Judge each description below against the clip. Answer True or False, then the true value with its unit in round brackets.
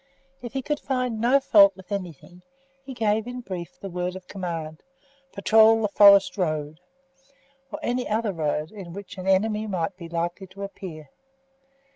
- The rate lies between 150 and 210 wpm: True (165 wpm)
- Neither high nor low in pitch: False (195 Hz)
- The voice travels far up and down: False (4.1 semitones)